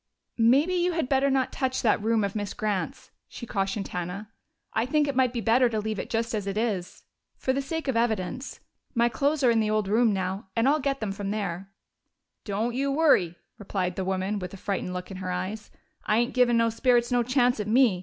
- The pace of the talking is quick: Yes, fast, 225 wpm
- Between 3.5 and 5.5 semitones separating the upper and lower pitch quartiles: Yes, average, 4.4 semitones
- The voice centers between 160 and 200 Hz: No, high, 225 Hz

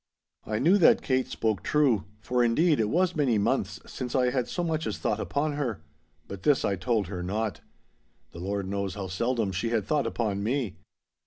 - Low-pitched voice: Yes, low, 115 Hz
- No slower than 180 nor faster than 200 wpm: Yes, average, 190 wpm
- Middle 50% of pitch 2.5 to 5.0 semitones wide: No, wide, 5.6 semitones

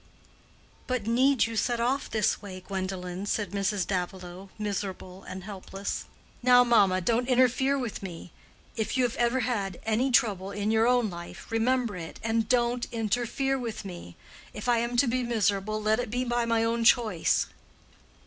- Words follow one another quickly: No, average, 170 wpm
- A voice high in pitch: Yes, high, 225 Hz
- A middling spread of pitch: Yes, average, 3.8 semitones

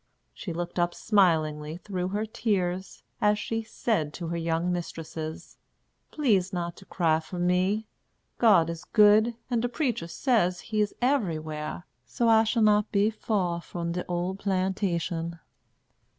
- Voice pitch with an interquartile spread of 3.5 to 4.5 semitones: Yes, average, 4.1 semitones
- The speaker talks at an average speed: Yes, average, 150 wpm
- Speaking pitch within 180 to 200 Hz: Yes, medium, 185 Hz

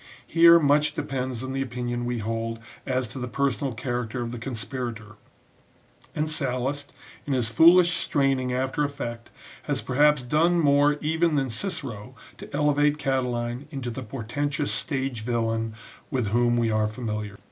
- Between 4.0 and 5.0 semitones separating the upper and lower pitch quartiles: No, average, 3.4 semitones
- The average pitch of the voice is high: No, low, 130 Hz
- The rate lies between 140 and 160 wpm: Yes, average, 150 wpm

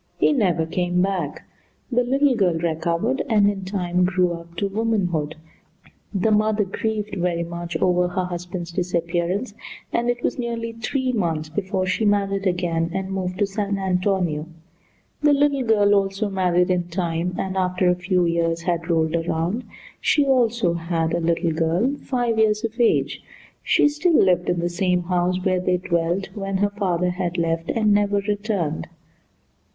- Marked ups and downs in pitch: No, average, 3.3 semitones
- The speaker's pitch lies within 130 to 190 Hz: Yes, medium, 185 Hz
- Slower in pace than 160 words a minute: No, average, 165 wpm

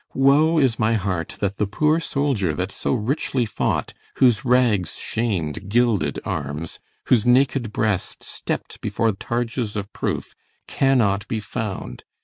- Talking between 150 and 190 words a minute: No, slow, 135 wpm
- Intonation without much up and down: No, average, 4.3 semitones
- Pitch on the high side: No, low, 110 Hz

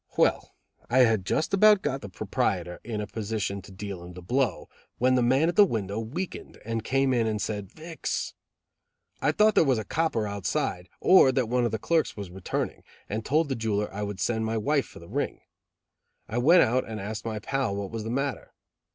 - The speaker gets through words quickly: Yes, fast, 210 wpm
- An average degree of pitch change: Yes, average, 4.8 semitones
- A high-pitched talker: No, low, 115 Hz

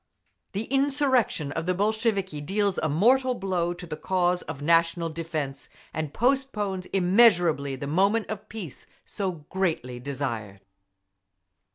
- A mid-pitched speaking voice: Yes, medium, 180 Hz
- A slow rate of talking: Yes, slow, 130 wpm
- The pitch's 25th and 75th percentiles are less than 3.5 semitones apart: No, wide, 5.5 semitones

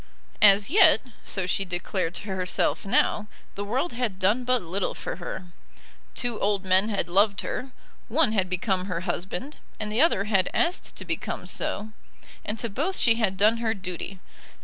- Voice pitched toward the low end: No, high, 205 Hz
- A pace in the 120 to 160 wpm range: No, average, 175 wpm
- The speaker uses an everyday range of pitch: Yes, average, 3.6 semitones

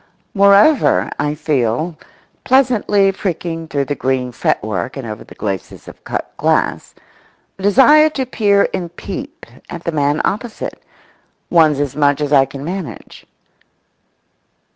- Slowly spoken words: Yes, slow, 130 wpm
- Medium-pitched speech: Yes, medium, 165 Hz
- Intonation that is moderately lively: No, wide, 6.3 semitones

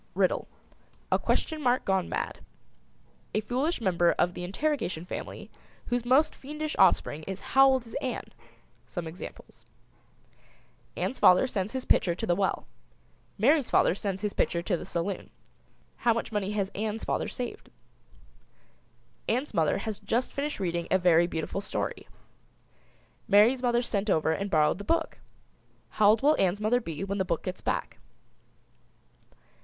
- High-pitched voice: Yes, high, 205 Hz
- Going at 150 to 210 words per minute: Yes, average, 155 wpm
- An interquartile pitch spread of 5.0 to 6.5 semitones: Yes, wide, 5.6 semitones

